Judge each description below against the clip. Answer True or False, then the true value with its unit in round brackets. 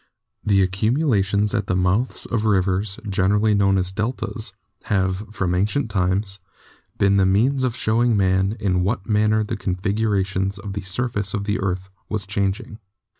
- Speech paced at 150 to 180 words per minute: True (155 wpm)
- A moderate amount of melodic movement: False (2.2 semitones)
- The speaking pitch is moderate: False (100 Hz)